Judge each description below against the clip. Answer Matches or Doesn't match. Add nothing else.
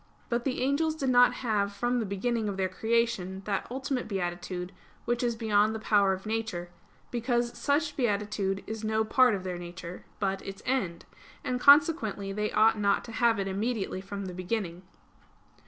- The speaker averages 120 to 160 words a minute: Doesn't match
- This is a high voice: Matches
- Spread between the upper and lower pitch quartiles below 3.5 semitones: Doesn't match